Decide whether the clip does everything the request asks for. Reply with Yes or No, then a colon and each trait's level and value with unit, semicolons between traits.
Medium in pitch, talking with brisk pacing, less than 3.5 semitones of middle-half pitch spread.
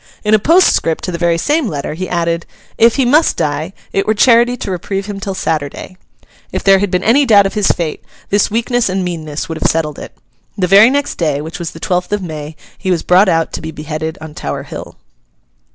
No: medium, 180 Hz; fast, 225 wpm; average, 4.5 semitones